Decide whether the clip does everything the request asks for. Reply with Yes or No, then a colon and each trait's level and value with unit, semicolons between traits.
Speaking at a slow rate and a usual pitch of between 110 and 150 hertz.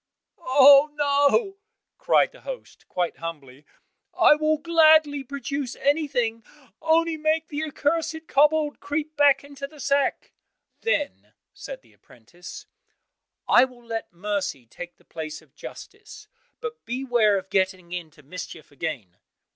No: slow, 130 wpm; very high, 280 Hz